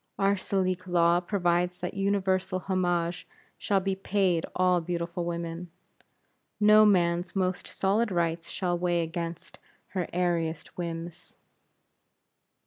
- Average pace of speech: No, slow, 115 wpm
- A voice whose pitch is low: No, medium, 180 Hz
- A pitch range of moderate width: No, narrow, 1.8 semitones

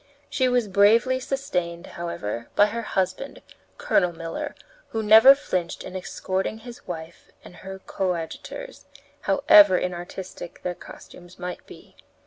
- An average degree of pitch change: Yes, average, 4.6 semitones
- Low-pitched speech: No, high, 190 Hz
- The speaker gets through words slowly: Yes, slow, 125 wpm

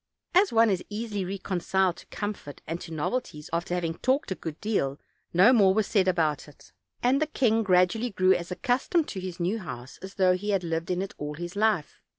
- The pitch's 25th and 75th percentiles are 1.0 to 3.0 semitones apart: No, average, 4.1 semitones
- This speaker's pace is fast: Yes, fast, 210 wpm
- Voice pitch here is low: No, high, 190 Hz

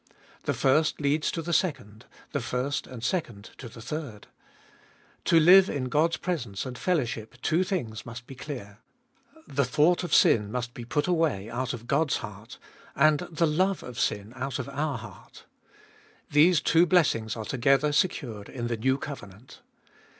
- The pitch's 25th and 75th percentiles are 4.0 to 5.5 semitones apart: Yes, average, 5.2 semitones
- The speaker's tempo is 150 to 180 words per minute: Yes, average, 165 wpm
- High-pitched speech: No, low, 135 Hz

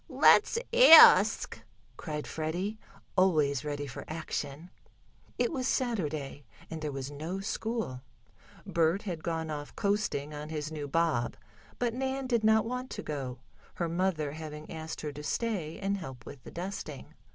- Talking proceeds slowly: No, average, 150 wpm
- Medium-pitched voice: Yes, medium, 160 Hz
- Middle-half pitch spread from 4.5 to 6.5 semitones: Yes, wide, 5.5 semitones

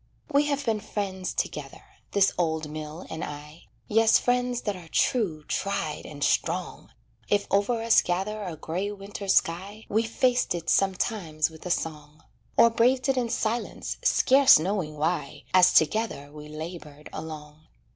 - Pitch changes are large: Yes, wide, 6.0 semitones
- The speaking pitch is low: No, medium, 185 Hz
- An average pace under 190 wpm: Yes, average, 155 wpm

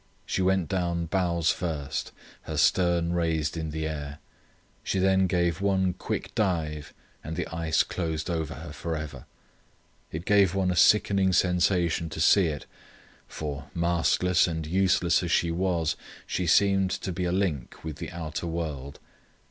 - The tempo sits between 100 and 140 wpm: No, average, 155 wpm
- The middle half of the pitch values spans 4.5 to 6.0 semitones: No, narrow, 2.6 semitones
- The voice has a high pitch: No, very low, 85 Hz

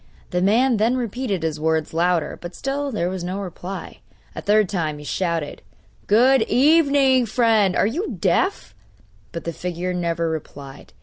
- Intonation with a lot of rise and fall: Yes, wide, 6.7 semitones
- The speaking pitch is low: No, high, 190 Hz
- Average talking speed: Yes, average, 160 wpm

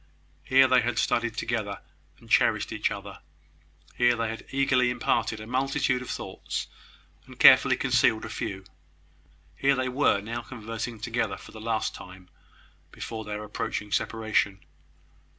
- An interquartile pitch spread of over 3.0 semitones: No, narrow, 2.5 semitones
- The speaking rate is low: No, average, 145 wpm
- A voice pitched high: No, low, 115 Hz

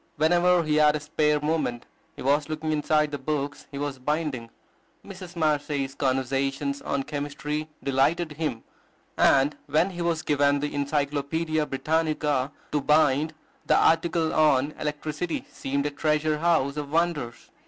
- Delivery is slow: No, average, 145 wpm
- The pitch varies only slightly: Yes, narrow, 1.9 semitones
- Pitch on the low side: No, medium, 150 Hz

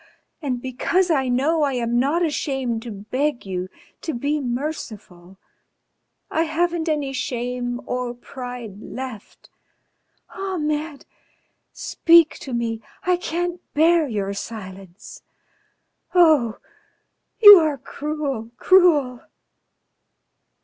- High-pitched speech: Yes, very high, 270 Hz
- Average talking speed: No, slow, 100 wpm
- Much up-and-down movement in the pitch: No, average, 5.0 semitones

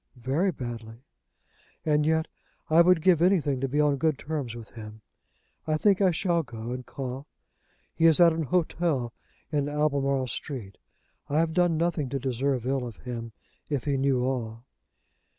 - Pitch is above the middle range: No, medium, 140 Hz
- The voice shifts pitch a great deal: No, average, 4.4 semitones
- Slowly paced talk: No, average, 170 wpm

